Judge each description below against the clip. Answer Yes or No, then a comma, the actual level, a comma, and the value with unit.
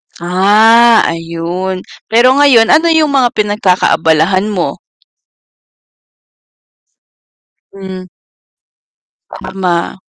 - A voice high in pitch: Yes, high, 195 Hz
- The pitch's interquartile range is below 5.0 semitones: Yes, average, 4.3 semitones